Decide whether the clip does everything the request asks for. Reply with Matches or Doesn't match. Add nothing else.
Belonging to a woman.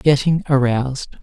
Doesn't match